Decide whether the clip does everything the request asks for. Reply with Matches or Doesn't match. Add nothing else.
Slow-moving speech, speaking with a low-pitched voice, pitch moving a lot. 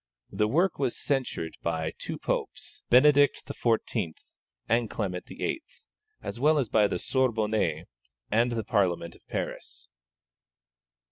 Matches